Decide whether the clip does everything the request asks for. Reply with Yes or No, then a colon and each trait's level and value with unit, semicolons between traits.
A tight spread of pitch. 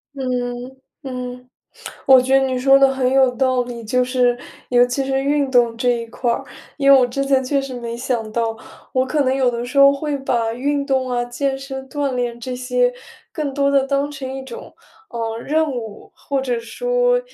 Yes: narrow, 2.0 semitones